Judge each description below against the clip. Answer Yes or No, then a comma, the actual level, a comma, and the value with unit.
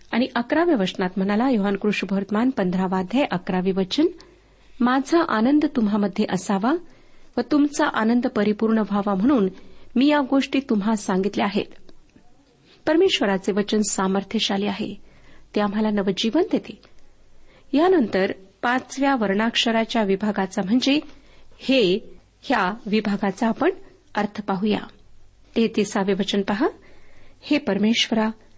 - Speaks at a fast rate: No, average, 105 wpm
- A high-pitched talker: Yes, high, 220 Hz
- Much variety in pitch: No, average, 4.8 semitones